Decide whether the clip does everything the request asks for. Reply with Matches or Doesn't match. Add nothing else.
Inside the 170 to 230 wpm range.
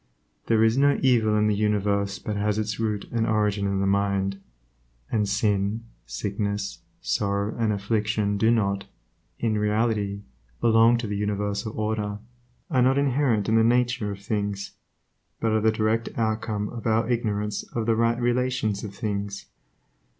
Doesn't match